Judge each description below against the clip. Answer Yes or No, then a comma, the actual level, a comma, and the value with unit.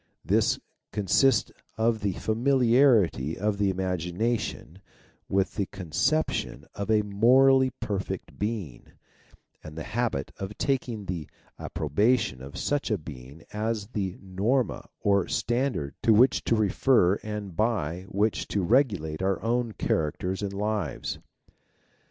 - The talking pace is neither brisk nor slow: No, slow, 130 wpm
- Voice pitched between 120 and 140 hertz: No, low, 105 Hz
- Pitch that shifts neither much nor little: Yes, average, 4.1 semitones